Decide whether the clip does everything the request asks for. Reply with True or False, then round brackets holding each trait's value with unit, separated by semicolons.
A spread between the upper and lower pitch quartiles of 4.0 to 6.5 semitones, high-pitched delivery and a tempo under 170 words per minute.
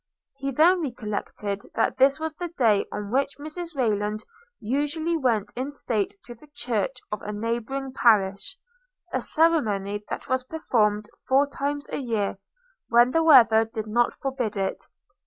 True (5.2 semitones; 245 Hz; 155 wpm)